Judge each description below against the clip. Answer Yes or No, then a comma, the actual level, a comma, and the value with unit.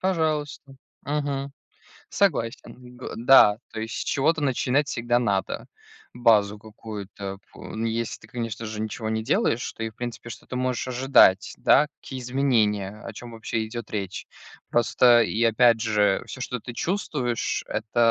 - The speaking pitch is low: Yes, low, 120 Hz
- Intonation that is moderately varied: Yes, average, 3.3 semitones